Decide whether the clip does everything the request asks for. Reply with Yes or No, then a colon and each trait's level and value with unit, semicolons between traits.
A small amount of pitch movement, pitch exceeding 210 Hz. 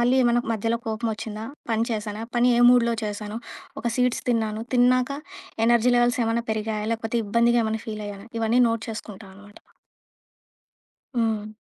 Yes: narrow, 1.8 semitones; high, 225 Hz